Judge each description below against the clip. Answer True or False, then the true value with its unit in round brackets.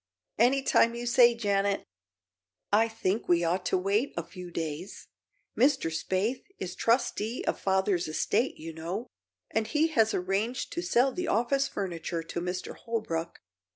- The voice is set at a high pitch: True (205 Hz)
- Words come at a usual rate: True (155 wpm)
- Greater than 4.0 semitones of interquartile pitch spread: True (5.1 semitones)